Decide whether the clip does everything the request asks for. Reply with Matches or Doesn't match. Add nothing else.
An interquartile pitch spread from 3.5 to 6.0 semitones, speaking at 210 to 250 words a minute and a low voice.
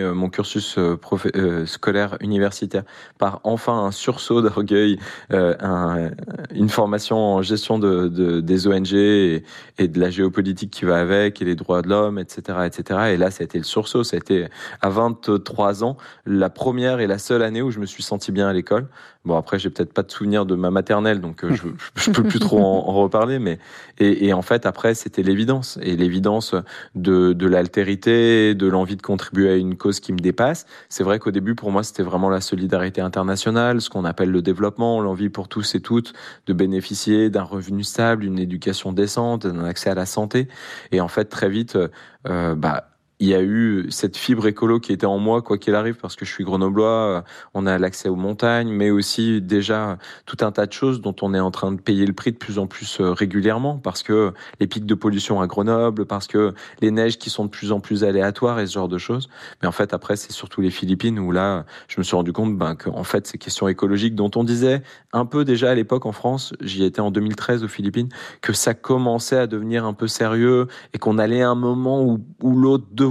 Doesn't match